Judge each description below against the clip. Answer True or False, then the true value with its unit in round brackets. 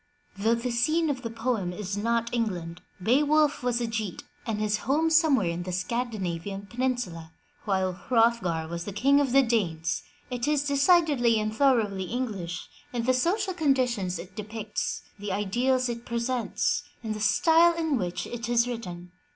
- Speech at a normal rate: True (165 wpm)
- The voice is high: True (230 Hz)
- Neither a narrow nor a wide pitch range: True (4.7 semitones)